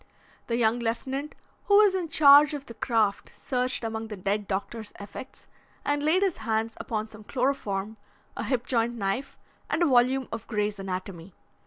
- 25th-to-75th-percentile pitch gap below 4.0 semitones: No, average, 4.5 semitones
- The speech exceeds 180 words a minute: No, average, 170 wpm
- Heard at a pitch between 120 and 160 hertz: No, high, 230 Hz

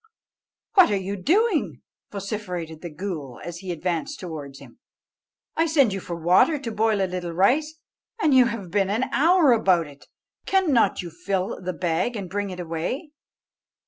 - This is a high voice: Yes, high, 195 Hz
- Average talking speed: Yes, average, 170 wpm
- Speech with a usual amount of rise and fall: No, wide, 6.5 semitones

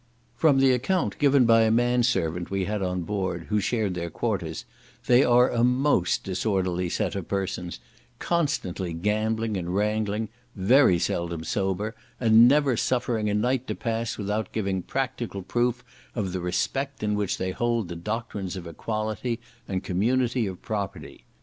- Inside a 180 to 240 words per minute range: No, average, 160 wpm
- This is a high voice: No, low, 105 Hz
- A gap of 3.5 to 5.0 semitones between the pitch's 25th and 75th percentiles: Yes, average, 4.5 semitones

